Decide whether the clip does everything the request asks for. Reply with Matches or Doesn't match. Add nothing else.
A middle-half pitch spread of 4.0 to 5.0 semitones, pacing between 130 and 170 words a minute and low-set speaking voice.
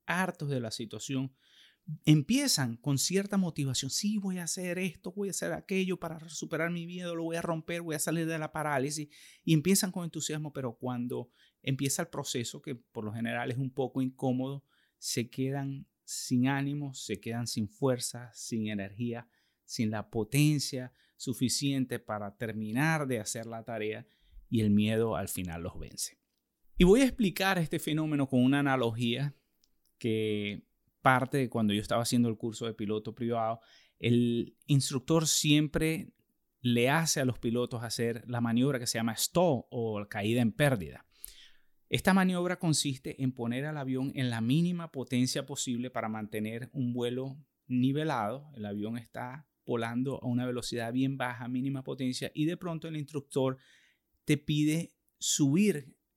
Matches